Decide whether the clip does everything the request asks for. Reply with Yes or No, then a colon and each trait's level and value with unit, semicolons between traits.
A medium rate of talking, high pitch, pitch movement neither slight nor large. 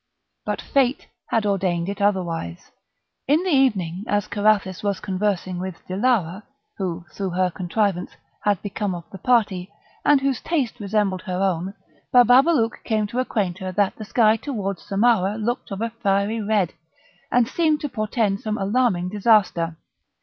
Yes: average, 155 wpm; high, 205 Hz; average, 3.5 semitones